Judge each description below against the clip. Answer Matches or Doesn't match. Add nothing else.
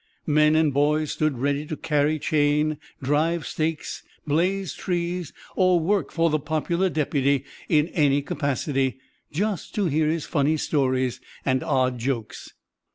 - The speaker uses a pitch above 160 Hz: Doesn't match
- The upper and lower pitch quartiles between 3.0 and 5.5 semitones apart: Doesn't match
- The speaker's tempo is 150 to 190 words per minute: Doesn't match